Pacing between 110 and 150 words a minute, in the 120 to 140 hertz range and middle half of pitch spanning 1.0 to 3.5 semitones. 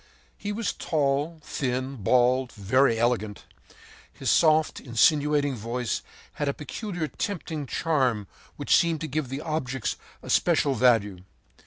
No: slow, 135 wpm; low, 135 Hz; average, 4.1 semitones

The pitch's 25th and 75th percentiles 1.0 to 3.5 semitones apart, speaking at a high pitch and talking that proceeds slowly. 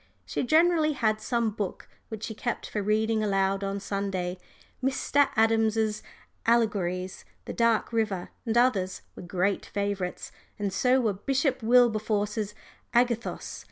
Yes: average, 3.1 semitones; high, 215 Hz; slow, 130 wpm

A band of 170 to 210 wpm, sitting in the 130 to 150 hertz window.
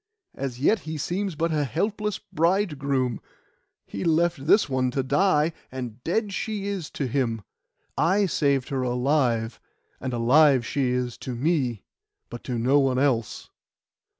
No: average, 150 wpm; medium, 140 Hz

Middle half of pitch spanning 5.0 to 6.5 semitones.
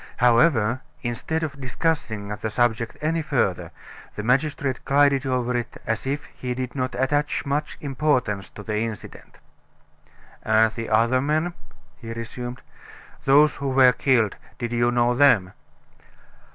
No: average, 3.6 semitones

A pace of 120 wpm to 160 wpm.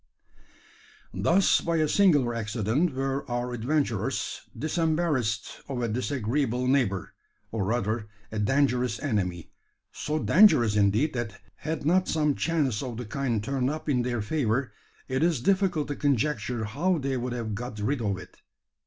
Yes: average, 150 wpm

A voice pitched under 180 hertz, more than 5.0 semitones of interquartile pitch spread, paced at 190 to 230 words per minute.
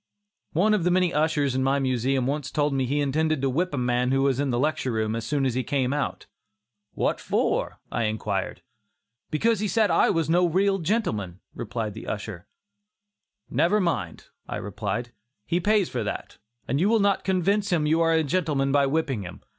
Yes: medium, 140 Hz; wide, 5.6 semitones; average, 195 wpm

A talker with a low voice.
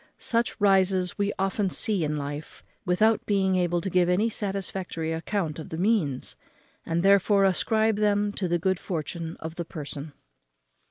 No: medium, 185 Hz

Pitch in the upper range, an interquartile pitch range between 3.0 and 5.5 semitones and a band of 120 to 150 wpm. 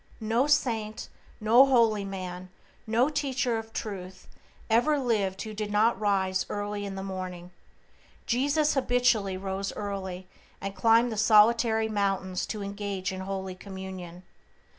Yes: high, 205 Hz; average, 3.3 semitones; slow, 135 wpm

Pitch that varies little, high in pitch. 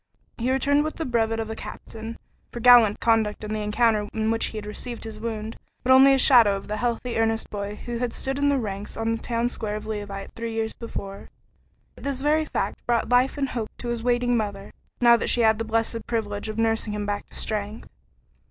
Yes: narrow, 2.3 semitones; high, 225 Hz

